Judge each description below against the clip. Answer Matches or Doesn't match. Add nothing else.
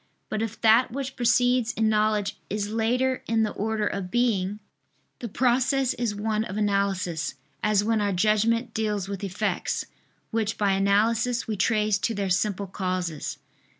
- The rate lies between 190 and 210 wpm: Doesn't match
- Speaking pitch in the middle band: Doesn't match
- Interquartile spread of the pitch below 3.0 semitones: Matches